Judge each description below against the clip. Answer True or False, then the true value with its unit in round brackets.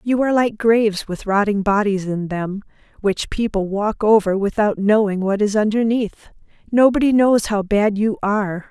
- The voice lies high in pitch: True (210 Hz)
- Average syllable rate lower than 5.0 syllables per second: True (4.8 syllables/s)